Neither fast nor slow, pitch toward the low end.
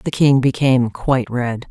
Yes: average, 175 wpm; low, 125 Hz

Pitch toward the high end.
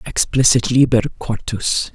No: low, 120 Hz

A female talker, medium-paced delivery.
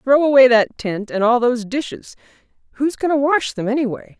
Yes: female; average, 185 wpm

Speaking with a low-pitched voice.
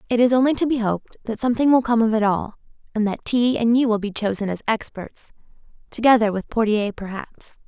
No: high, 225 Hz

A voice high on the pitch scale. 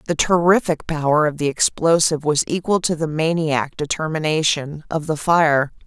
No: medium, 155 Hz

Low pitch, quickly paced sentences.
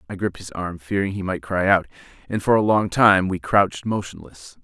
Yes: very low, 95 Hz; fast, 220 wpm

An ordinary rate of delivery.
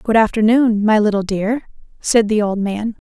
Yes: average, 175 wpm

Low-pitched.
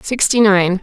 No: high, 205 Hz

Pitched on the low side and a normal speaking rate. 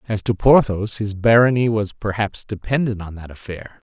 Yes: low, 105 Hz; average, 170 wpm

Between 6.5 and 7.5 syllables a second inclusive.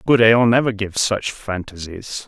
No: 5.2 syllables/s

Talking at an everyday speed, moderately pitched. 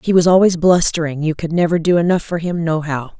No: fast, 245 wpm; medium, 165 Hz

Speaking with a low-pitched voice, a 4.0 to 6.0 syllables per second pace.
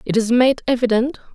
No: high, 240 Hz; 5.8 syllables/s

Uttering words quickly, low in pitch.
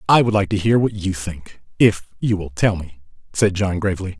Yes: fast, 230 wpm; very low, 95 Hz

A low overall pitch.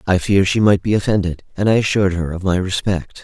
Yes: very low, 95 Hz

